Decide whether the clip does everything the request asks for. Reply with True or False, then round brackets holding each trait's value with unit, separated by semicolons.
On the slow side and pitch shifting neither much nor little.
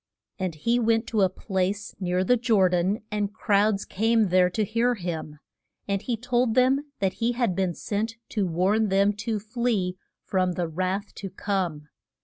False (175 wpm; 3.5 semitones)